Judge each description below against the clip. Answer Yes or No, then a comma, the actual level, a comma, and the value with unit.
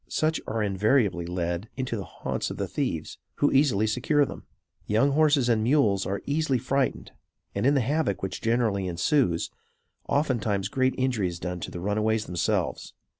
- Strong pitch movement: Yes, wide, 5.8 semitones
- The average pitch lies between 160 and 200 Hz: No, low, 110 Hz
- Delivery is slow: No, average, 170 wpm